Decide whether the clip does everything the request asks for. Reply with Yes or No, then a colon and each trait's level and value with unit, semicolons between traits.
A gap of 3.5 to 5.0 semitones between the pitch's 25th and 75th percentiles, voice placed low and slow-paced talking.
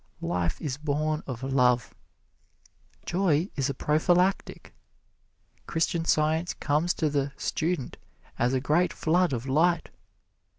No: average, 3.9 semitones; medium, 155 Hz; slow, 120 wpm